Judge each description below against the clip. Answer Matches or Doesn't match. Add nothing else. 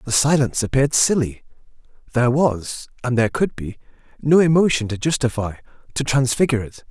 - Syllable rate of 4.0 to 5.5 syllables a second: Doesn't match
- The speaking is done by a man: Matches